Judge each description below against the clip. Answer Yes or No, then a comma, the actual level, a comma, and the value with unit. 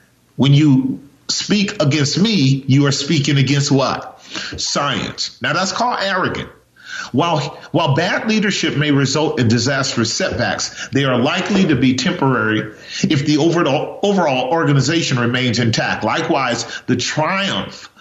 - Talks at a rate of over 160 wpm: No, slow, 135 wpm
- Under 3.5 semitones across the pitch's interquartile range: No, average, 4.6 semitones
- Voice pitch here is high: No, medium, 145 Hz